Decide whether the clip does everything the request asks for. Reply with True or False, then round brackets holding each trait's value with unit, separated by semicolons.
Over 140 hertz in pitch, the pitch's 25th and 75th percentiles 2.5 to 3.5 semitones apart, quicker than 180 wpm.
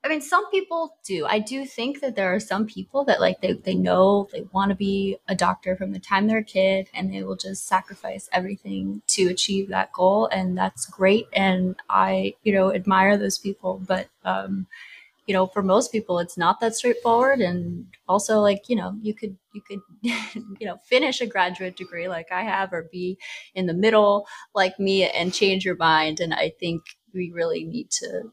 True (190 Hz; 3.0 semitones; 205 wpm)